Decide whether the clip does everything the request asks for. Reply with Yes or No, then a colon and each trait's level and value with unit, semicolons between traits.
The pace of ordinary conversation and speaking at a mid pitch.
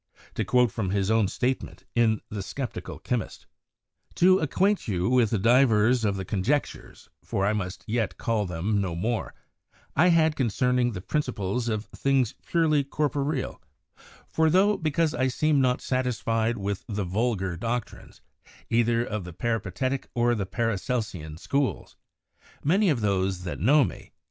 No: average, 150 wpm; low, 120 Hz